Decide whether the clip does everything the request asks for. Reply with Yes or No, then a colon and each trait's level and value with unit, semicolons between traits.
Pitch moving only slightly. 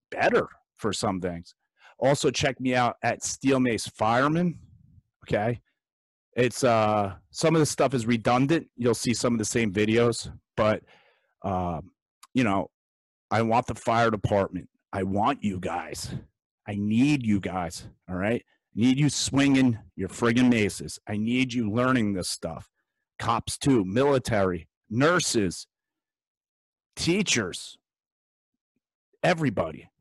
No: average, 4.3 semitones